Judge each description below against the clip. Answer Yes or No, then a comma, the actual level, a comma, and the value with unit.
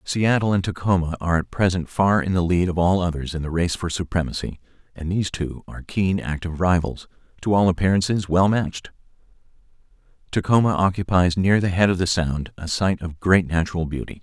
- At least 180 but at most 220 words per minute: Yes, average, 185 wpm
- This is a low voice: Yes, very low, 90 Hz